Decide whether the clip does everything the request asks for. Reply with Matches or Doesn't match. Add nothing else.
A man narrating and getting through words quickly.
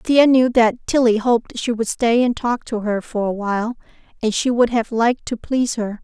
Doesn't match